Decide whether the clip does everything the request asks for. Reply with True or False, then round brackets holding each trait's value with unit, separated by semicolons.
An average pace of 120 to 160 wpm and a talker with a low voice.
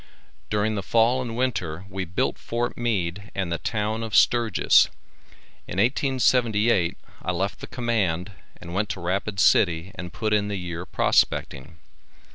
True (150 wpm; 105 Hz)